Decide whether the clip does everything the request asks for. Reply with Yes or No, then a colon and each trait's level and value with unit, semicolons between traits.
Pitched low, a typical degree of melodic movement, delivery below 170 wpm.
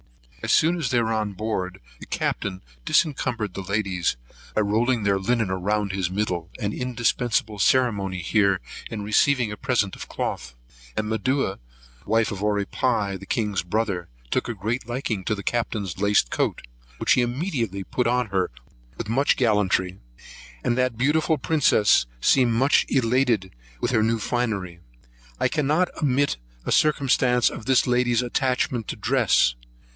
Yes: low, 110 Hz; average, 4.1 semitones; average, 155 wpm